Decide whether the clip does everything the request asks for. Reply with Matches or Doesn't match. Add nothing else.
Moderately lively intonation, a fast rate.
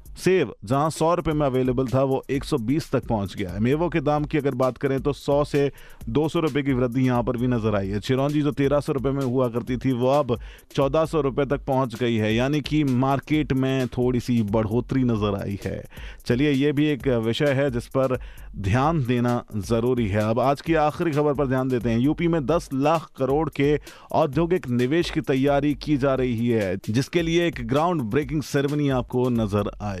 Matches